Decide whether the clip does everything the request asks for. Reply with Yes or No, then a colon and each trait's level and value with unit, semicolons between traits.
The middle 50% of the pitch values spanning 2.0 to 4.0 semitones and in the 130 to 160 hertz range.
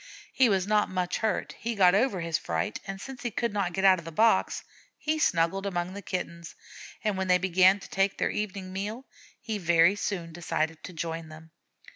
No: average, 3.3 semitones; high, 190 Hz